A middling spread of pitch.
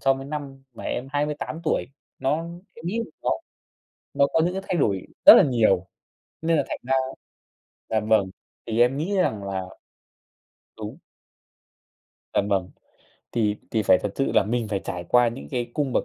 No: wide, 5.8 semitones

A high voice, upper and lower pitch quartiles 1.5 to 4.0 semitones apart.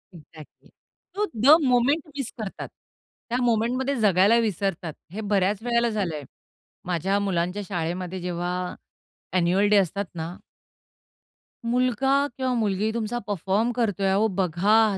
No: high, 205 Hz; average, 4.5 semitones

